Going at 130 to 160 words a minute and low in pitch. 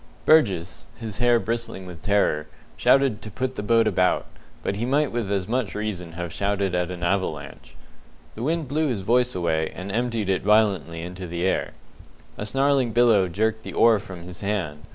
No: average, 185 wpm; low, 100 Hz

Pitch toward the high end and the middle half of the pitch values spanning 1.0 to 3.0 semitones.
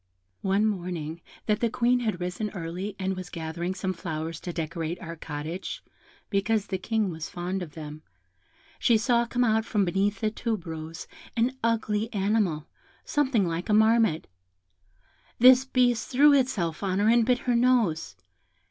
No: high, 195 Hz; average, 5.1 semitones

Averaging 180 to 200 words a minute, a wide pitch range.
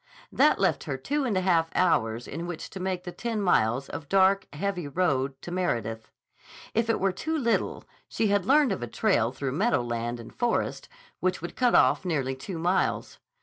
Yes: average, 190 wpm; wide, 6.9 semitones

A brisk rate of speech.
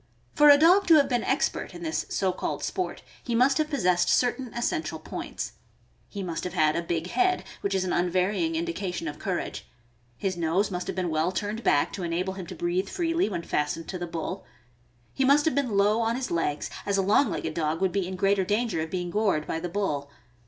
Yes: fast, 220 wpm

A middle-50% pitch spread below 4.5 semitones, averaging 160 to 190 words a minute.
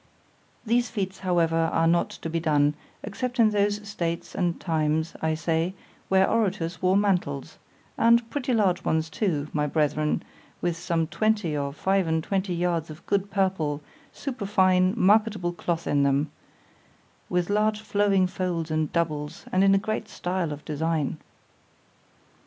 No: average, 3.9 semitones; average, 145 wpm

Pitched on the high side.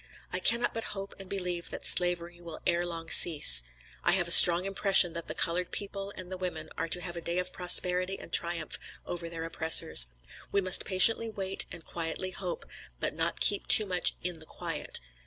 No: medium, 180 Hz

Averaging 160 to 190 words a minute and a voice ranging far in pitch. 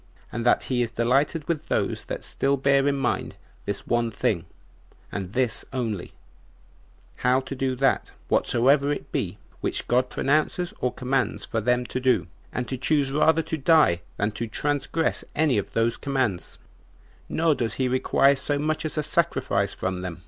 No: average, 170 wpm; average, 3.5 semitones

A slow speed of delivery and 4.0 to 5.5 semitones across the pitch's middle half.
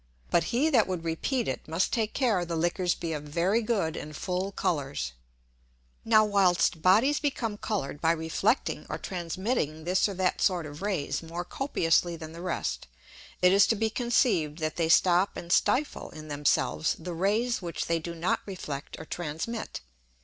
No: average, 175 wpm; average, 4.5 semitones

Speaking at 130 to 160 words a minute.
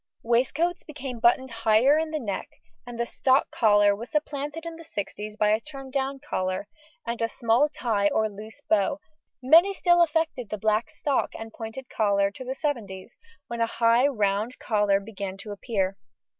No: average, 170 wpm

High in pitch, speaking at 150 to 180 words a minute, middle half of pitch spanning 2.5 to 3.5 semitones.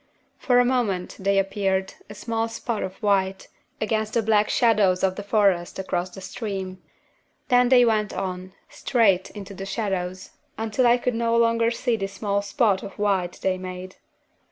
Yes: high, 200 Hz; average, 170 wpm; average, 3.2 semitones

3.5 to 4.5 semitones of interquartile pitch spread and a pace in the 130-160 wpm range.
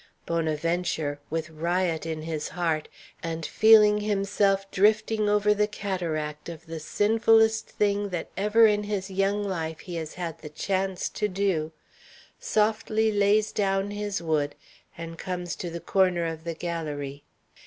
Yes: average, 4.1 semitones; average, 145 wpm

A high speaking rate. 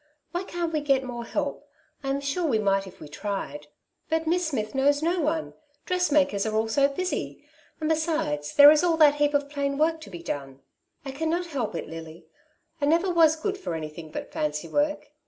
Yes: fast, 210 wpm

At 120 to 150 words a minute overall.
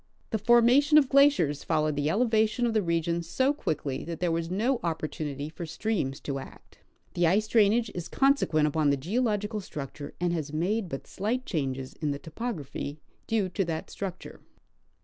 No: average, 175 wpm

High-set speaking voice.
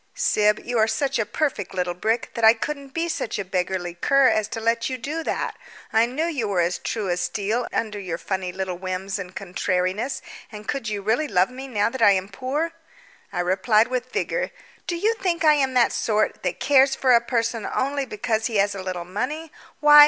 Yes: high, 225 Hz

